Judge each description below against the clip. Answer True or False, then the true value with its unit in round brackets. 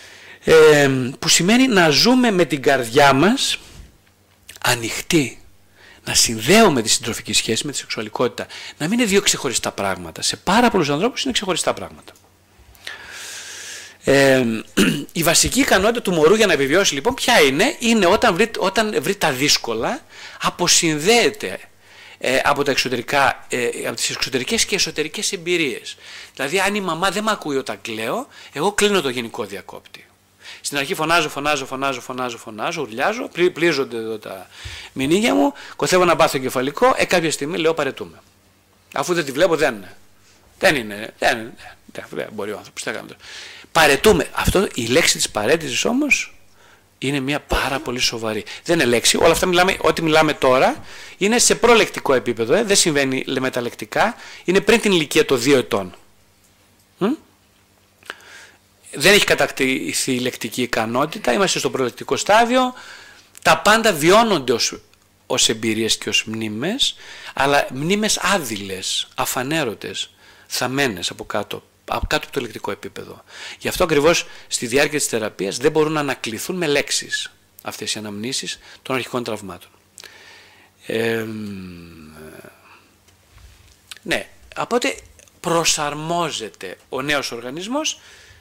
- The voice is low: False (145 Hz)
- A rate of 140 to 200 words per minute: True (145 wpm)